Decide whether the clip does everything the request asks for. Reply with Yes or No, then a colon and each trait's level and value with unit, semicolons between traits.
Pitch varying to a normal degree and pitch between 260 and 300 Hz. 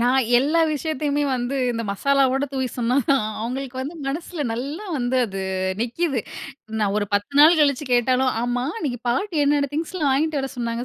Yes: average, 3.3 semitones; very high, 265 Hz